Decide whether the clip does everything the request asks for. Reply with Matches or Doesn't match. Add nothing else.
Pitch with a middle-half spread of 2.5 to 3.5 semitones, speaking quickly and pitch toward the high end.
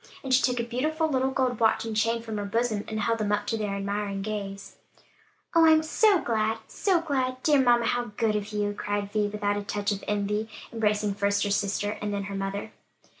Matches